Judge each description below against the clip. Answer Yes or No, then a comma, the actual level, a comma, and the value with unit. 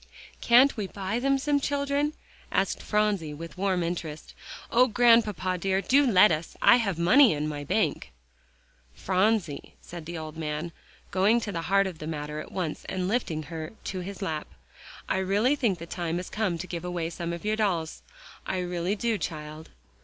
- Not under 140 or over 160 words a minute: No, average, 185 wpm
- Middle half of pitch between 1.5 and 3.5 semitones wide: No, average, 4.6 semitones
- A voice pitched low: No, medium, 185 Hz